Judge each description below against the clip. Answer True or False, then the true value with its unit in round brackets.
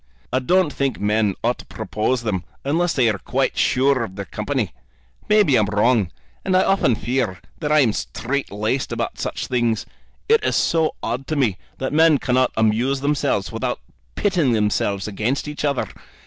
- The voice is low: True (130 Hz)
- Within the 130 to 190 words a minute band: True (175 wpm)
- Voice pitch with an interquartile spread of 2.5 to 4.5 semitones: False (5.4 semitones)